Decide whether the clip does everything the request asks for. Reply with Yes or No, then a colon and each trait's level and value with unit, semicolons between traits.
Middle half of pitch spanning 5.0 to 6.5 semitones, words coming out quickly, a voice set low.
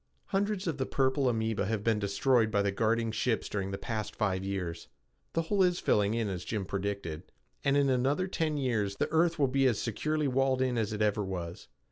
Yes: wide, 5.4 semitones; fast, 210 wpm; low, 115 Hz